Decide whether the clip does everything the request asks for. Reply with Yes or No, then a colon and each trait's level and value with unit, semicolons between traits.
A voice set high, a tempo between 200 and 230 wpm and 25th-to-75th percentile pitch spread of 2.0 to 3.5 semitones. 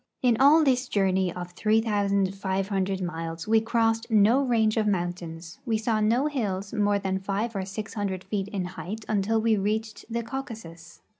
No: high, 205 Hz; average, 170 wpm; average, 3.0 semitones